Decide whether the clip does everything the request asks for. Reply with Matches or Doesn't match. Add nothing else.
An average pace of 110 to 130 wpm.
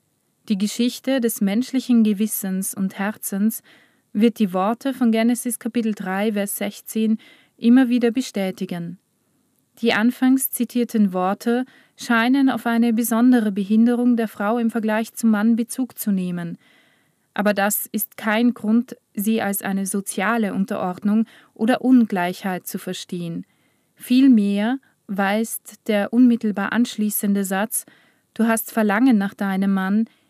Matches